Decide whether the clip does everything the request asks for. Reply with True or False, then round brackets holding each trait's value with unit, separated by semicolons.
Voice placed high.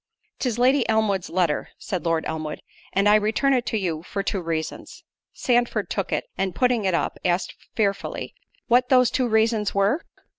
True (210 Hz)